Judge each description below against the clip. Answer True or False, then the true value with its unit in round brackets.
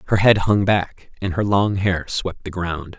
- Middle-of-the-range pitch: False (95 Hz)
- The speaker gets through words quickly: True (220 wpm)